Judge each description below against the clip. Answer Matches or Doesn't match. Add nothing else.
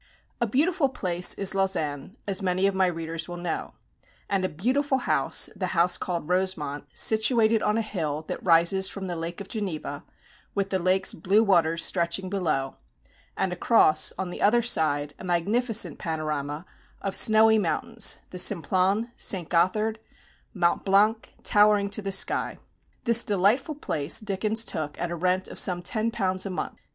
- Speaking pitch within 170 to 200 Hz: Matches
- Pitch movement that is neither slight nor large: Matches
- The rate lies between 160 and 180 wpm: Matches